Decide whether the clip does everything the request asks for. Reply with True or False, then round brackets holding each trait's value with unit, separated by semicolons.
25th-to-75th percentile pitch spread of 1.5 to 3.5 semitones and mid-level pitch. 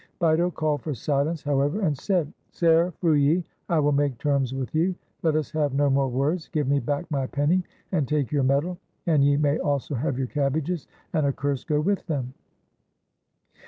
True (2.5 semitones; 145 Hz)